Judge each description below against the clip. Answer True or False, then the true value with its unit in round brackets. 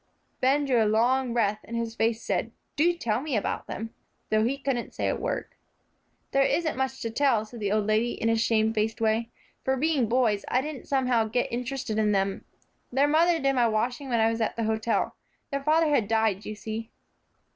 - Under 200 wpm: False (205 wpm)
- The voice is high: True (235 Hz)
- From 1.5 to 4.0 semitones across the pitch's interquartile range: True (3.4 semitones)